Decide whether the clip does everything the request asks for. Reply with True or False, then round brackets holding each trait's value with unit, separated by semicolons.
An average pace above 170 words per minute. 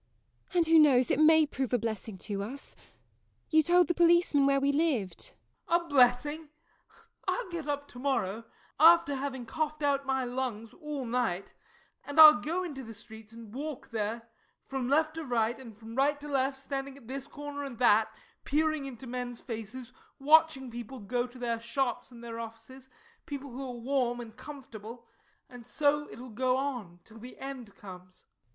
True (185 wpm)